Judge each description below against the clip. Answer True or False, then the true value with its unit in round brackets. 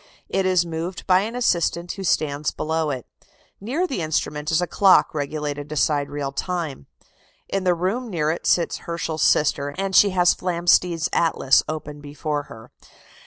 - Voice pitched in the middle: True (165 Hz)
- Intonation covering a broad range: False (3.6 semitones)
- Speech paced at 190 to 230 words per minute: False (165 wpm)